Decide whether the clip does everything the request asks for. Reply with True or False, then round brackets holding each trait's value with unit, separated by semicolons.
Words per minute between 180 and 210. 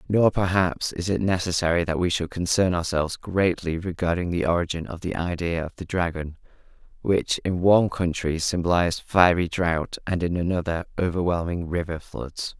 False (155 wpm)